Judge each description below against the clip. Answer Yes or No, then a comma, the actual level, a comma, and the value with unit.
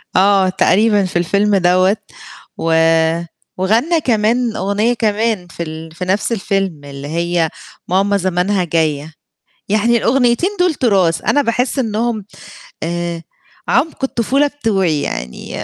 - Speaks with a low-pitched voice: No, high, 200 Hz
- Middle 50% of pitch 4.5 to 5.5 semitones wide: Yes, average, 5.1 semitones